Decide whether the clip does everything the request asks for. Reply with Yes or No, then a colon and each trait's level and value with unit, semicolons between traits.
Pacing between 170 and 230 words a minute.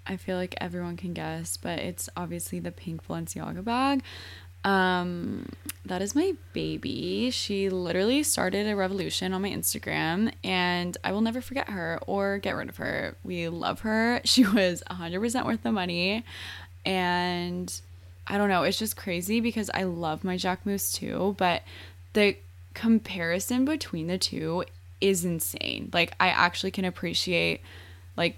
No: average, 160 wpm